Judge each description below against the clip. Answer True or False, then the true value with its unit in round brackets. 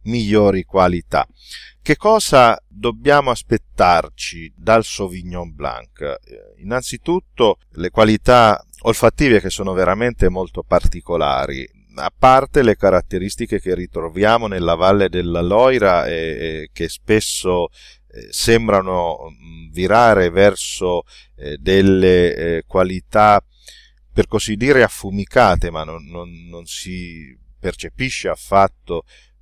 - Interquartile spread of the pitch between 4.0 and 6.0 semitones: True (4.7 semitones)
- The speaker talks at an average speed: False (105 wpm)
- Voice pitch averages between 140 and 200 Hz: False (95 Hz)